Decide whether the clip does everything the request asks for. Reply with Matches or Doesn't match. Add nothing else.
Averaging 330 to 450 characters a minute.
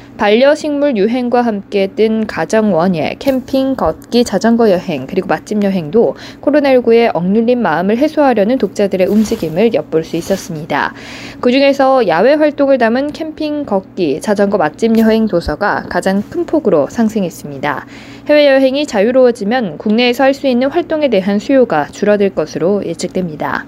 Matches